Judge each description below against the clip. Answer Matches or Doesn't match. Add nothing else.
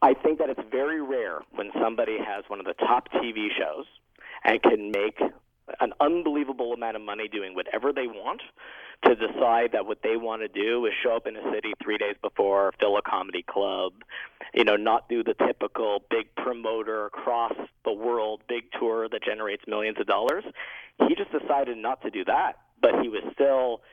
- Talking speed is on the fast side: Doesn't match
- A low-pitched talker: Matches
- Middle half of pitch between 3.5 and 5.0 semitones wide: Doesn't match